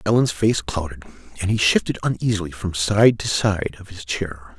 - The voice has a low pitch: Yes, very low, 95 Hz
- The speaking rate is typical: Yes, average, 185 wpm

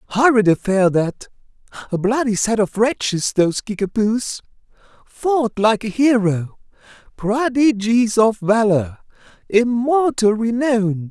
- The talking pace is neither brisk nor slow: No, slow, 80 wpm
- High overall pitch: Yes, high, 220 Hz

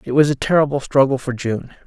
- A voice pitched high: No, low, 135 Hz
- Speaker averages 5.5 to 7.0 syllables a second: Yes, 5.9 syllables/s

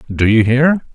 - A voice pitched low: Yes, low, 125 Hz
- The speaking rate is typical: Yes, average, 190 wpm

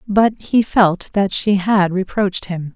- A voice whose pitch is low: No, high, 195 Hz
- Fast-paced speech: No, average, 175 wpm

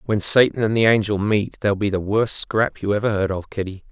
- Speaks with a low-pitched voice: Yes, low, 105 Hz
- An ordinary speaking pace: No, fast, 245 wpm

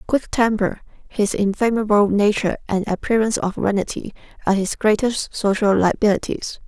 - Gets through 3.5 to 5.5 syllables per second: Yes, 5.4 syllables/s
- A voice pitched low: No, high, 210 Hz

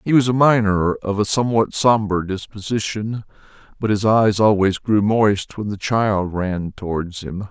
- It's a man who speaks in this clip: Yes, male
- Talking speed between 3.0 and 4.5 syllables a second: Yes, 4.4 syllables/s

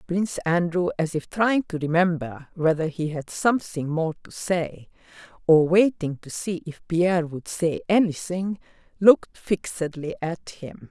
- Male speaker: No, female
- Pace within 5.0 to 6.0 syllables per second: No, 4.4 syllables/s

